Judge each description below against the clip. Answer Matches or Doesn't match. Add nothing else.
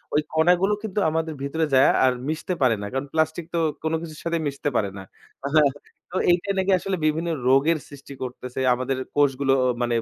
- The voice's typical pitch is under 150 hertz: Doesn't match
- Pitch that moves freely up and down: Doesn't match